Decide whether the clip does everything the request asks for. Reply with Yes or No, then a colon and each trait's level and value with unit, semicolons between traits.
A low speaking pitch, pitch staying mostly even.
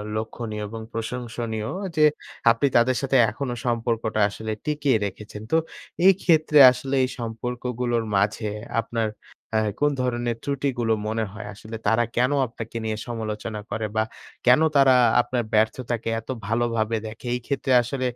Yes: low, 115 Hz; narrow, 2.3 semitones